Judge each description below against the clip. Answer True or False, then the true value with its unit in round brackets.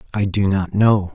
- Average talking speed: False (210 wpm)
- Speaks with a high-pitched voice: False (100 Hz)